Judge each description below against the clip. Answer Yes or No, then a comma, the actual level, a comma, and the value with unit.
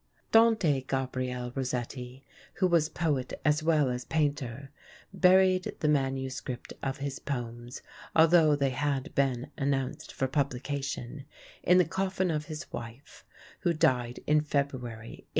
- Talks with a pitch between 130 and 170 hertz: Yes, medium, 140 Hz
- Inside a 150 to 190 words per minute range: No, slow, 135 wpm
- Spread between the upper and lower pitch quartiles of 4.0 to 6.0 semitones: No, average, 3.3 semitones